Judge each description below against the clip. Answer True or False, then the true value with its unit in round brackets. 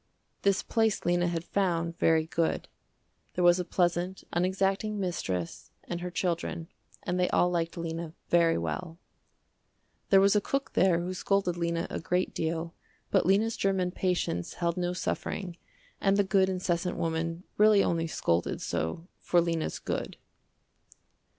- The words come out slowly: False (150 wpm)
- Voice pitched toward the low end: False (175 Hz)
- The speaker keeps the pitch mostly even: True (2.2 semitones)